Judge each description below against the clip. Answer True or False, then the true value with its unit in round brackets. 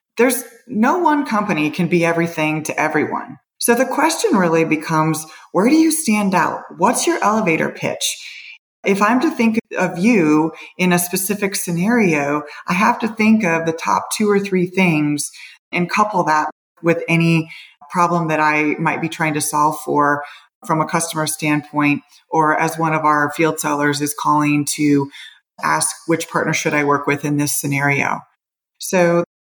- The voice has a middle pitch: True (165 Hz)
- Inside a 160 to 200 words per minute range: True (170 wpm)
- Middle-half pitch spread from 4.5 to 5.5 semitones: True (5.2 semitones)